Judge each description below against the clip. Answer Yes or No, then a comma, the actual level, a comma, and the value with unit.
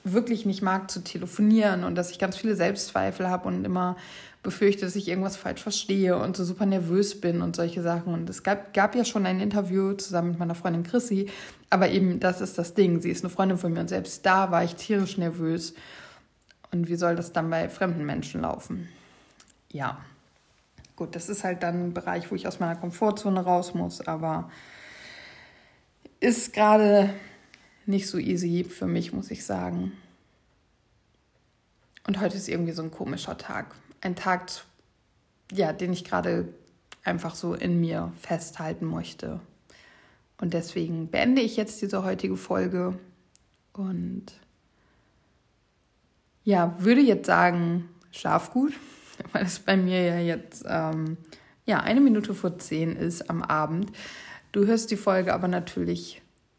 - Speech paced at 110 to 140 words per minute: No, average, 160 wpm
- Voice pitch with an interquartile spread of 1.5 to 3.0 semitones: Yes, average, 2.7 semitones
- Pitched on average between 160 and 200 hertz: Yes, medium, 185 Hz